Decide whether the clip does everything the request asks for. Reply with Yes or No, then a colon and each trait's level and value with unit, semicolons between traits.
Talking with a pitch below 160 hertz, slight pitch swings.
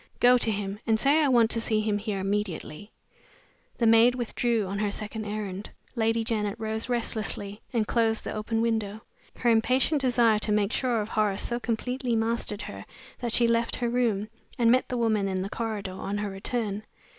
No: high, 220 Hz; narrow, 2.2 semitones